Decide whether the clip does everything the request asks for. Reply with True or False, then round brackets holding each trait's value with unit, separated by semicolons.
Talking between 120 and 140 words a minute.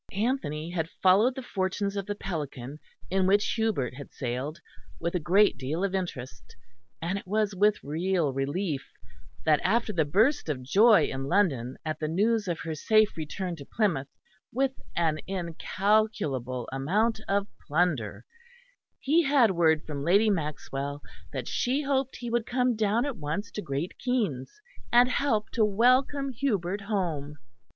False (155 wpm)